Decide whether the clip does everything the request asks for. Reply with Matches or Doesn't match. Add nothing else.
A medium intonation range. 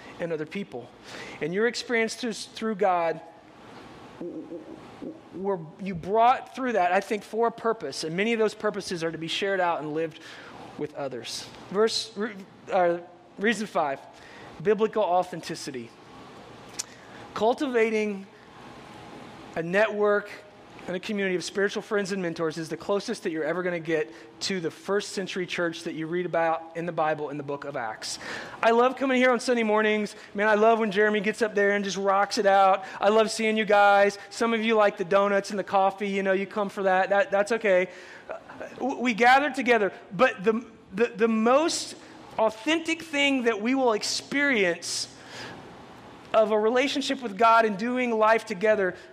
Matches